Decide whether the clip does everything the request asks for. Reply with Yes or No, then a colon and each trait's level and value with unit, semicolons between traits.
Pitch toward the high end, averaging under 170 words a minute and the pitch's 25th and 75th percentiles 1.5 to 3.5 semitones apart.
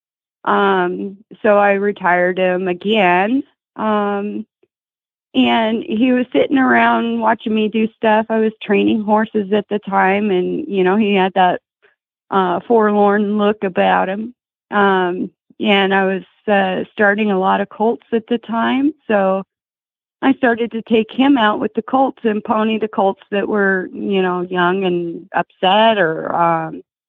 Yes: high, 210 Hz; average, 155 wpm; average, 2.8 semitones